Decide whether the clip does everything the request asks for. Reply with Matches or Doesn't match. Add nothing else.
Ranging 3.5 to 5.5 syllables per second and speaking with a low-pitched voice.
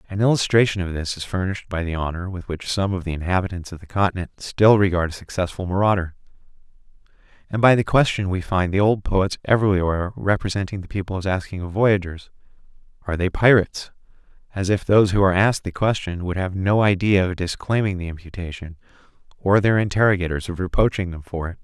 Doesn't match